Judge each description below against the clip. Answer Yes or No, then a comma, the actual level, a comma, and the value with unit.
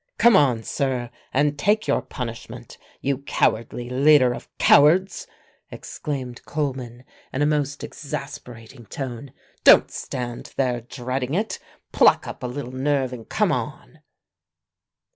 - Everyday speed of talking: No, slow, 125 wpm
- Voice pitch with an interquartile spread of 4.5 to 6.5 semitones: No, average, 2.9 semitones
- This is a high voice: No, low, 130 Hz